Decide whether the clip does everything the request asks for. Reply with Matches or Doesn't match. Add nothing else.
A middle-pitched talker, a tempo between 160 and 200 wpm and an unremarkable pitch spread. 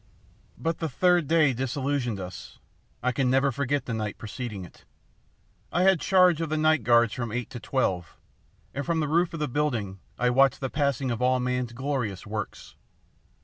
Doesn't match